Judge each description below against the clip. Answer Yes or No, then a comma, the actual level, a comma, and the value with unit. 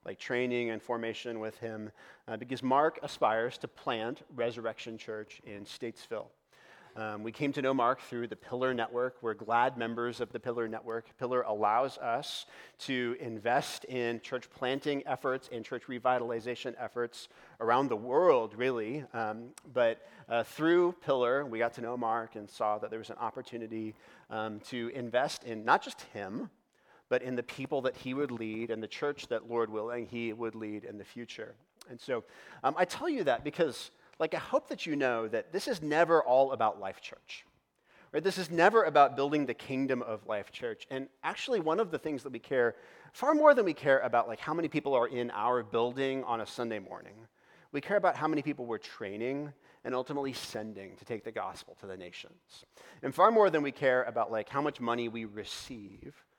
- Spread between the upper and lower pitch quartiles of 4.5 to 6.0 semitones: No, average, 3.1 semitones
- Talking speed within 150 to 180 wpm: No, average, 195 wpm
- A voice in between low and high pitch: No, low, 120 Hz